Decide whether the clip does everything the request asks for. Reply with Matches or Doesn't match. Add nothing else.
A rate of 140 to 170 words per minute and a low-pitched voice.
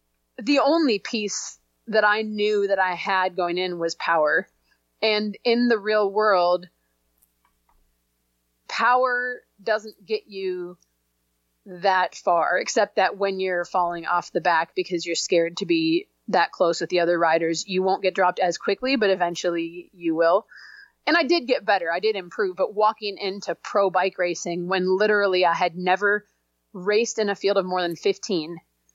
Doesn't match